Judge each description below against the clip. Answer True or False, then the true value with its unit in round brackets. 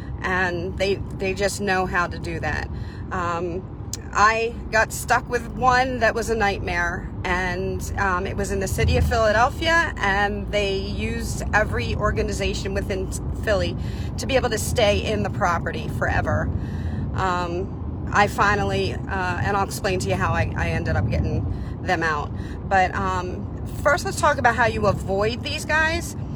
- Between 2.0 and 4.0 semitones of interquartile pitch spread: False (4.6 semitones)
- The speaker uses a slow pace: False (165 wpm)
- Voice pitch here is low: False (205 Hz)